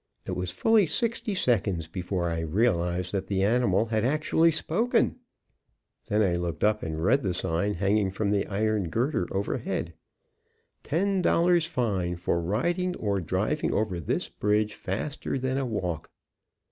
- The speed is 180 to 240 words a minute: No, average, 150 wpm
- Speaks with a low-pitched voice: Yes, low, 105 Hz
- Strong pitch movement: Yes, wide, 7.0 semitones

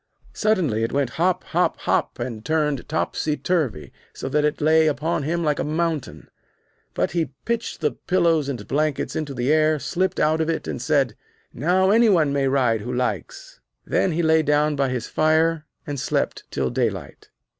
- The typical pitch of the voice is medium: Yes, medium, 155 Hz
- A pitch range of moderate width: Yes, average, 3.3 semitones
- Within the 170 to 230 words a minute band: Yes, average, 180 wpm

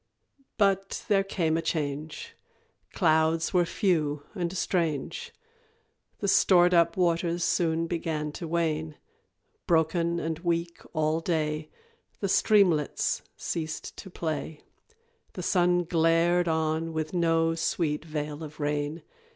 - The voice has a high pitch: No, medium, 165 Hz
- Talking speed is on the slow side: Yes, slow, 120 wpm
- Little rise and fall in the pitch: Yes, narrow, 1.9 semitones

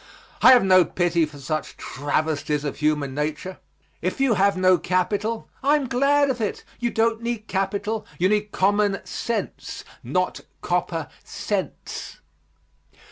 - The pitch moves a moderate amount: No, wide, 6.2 semitones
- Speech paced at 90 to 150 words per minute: Yes, average, 140 wpm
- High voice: Yes, high, 195 Hz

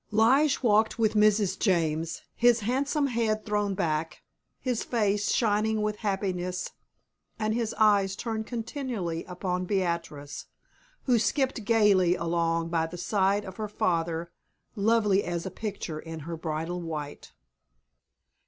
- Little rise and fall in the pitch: No, average, 4.5 semitones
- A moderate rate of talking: No, slow, 130 wpm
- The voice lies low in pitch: No, high, 200 Hz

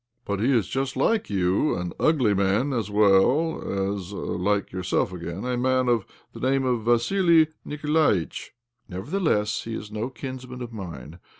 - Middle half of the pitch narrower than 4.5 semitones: No, average, 5.2 semitones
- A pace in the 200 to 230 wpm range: No, average, 170 wpm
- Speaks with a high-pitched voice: No, low, 115 Hz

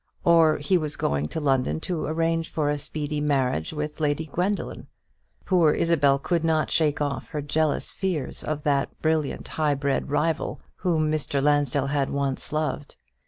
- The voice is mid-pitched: Yes, medium, 150 Hz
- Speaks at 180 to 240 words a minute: No, average, 165 wpm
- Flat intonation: Yes, narrow, 2.1 semitones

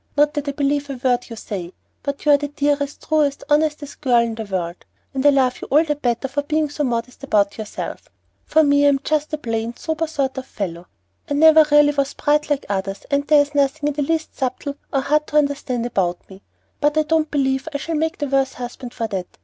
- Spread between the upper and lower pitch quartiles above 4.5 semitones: No, average, 3.4 semitones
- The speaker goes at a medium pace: No, fast, 230 wpm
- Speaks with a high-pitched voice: Yes, very high, 280 Hz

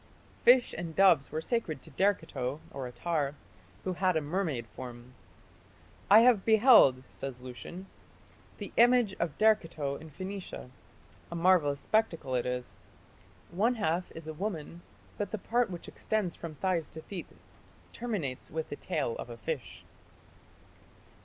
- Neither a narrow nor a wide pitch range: No, wide, 6.2 semitones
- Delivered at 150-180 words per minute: No, average, 140 wpm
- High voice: No, medium, 165 Hz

